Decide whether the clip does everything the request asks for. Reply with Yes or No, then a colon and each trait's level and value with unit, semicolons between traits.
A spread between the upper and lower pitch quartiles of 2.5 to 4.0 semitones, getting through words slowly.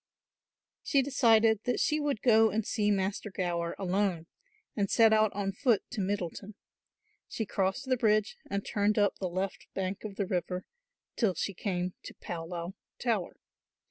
No: average, 2.9 semitones; average, 165 wpm